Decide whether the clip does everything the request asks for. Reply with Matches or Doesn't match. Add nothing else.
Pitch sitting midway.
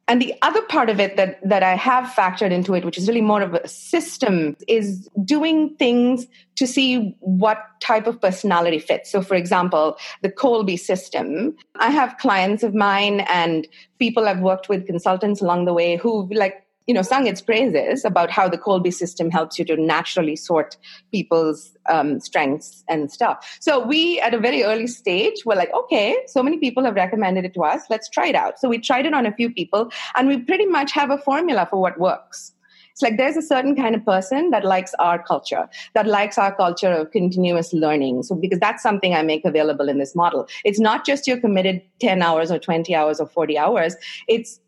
Doesn't match